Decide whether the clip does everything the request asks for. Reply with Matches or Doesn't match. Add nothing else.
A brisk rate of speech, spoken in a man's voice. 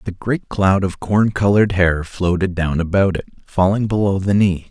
Doesn't match